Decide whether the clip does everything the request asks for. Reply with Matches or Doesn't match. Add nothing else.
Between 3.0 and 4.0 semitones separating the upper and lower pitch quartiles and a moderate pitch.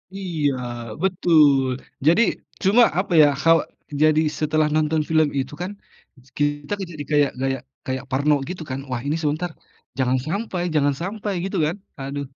Matches